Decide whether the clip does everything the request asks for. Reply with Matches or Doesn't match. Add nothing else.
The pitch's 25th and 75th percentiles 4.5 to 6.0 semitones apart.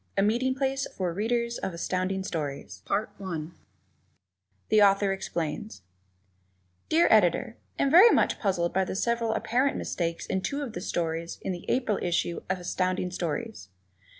Matches